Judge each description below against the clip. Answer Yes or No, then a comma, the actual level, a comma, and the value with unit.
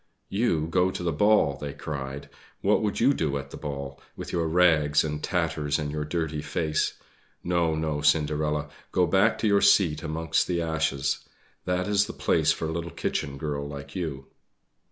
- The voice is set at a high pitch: No, very low, 80 Hz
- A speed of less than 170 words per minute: No, average, 180 wpm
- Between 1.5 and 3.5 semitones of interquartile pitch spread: Yes, average, 3.1 semitones